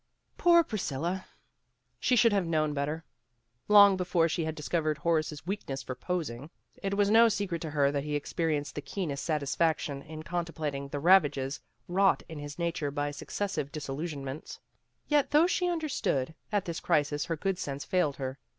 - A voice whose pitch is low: No, medium, 160 Hz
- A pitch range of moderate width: Yes, average, 4.6 semitones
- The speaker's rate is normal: Yes, average, 170 wpm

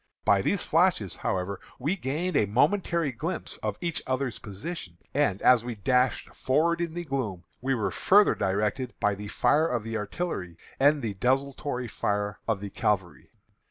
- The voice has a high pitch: No, low, 125 Hz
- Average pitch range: No, wide, 6.9 semitones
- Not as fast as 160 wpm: No, average, 165 wpm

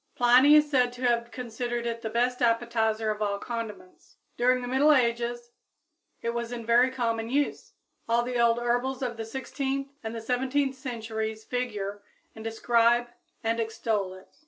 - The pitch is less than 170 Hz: No, high, 235 Hz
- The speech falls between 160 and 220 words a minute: Yes, average, 165 wpm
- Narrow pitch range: Yes, narrow, 1.8 semitones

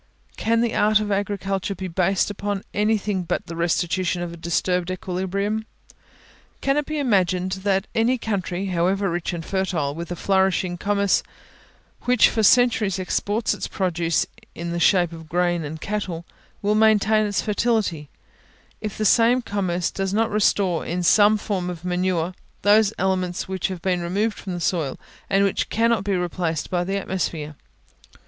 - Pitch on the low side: No, high, 190 Hz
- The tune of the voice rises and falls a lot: No, average, 2.9 semitones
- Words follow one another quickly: No, average, 165 wpm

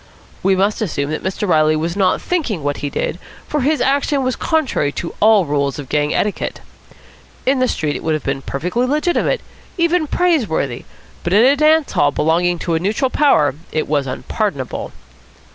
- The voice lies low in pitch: No, high, 190 Hz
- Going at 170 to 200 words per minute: Yes, average, 180 wpm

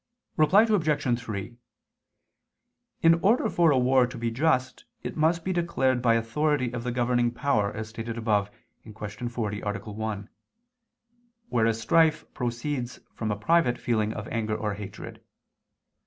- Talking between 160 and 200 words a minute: No, average, 145 wpm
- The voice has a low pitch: Yes, low, 120 Hz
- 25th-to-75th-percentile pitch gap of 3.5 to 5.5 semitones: Yes, average, 5.0 semitones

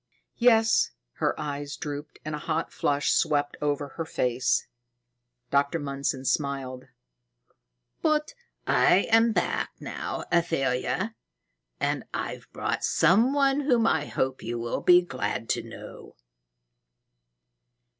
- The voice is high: No, medium, 150 Hz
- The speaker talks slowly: Yes, slow, 115 wpm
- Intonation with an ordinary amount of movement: No, wide, 7.9 semitones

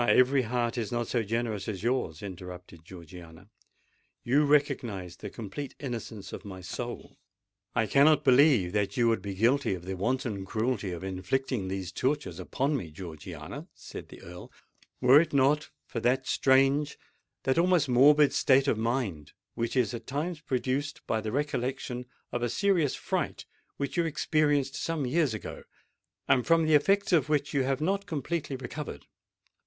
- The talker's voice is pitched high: No, low, 125 Hz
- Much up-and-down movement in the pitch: Yes, wide, 6.1 semitones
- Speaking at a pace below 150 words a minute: No, average, 160 wpm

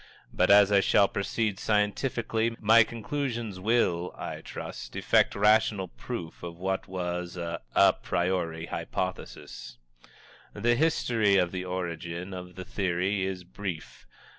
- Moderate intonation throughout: Yes, average, 3.6 semitones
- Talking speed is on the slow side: Yes, slow, 130 wpm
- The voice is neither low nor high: No, very low, 95 Hz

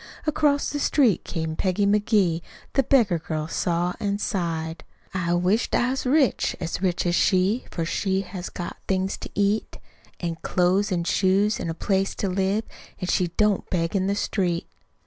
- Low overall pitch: No, high, 190 Hz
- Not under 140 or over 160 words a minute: No, average, 175 wpm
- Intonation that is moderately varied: Yes, average, 3.1 semitones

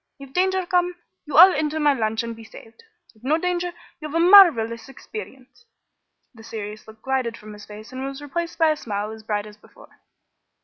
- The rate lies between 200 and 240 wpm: Yes, fast, 205 wpm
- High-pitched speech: Yes, very high, 265 Hz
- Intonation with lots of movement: Yes, wide, 6.9 semitones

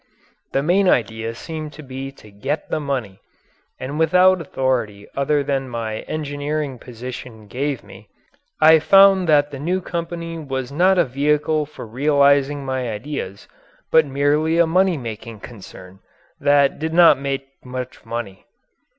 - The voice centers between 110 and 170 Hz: Yes, medium, 140 Hz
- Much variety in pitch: No, average, 3.9 semitones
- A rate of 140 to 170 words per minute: Yes, average, 150 wpm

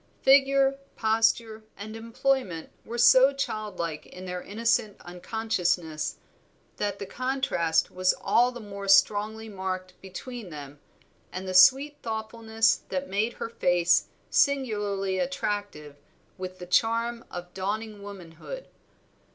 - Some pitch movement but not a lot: Yes, average, 4.0 semitones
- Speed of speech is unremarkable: No, slow, 120 wpm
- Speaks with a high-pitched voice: Yes, high, 205 Hz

